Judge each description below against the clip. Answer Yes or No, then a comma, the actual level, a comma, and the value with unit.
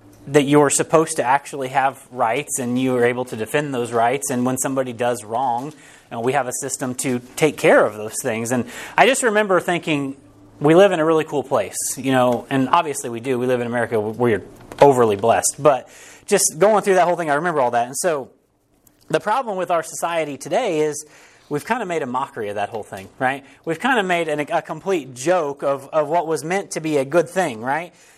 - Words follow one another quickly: Yes, fast, 240 wpm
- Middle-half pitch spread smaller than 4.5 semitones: No, average, 4.8 semitones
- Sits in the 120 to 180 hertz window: Yes, medium, 140 Hz